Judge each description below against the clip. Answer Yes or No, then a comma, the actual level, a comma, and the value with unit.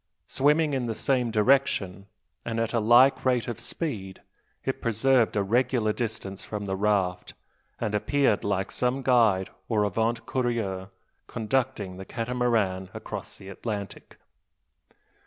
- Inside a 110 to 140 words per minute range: Yes, slow, 135 wpm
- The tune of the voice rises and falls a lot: No, average, 3.8 semitones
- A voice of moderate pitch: No, low, 115 Hz